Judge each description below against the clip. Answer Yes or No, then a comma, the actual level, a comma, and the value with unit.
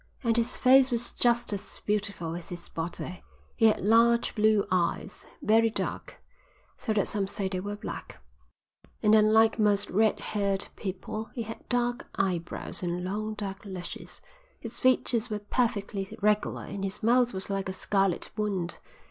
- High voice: Yes, high, 210 Hz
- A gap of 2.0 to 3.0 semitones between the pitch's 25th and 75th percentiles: Yes, average, 2.7 semitones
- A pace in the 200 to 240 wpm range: No, average, 160 wpm